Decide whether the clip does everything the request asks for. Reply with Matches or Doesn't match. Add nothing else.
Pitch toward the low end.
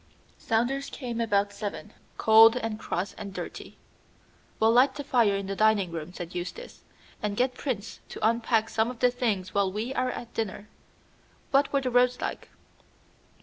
Doesn't match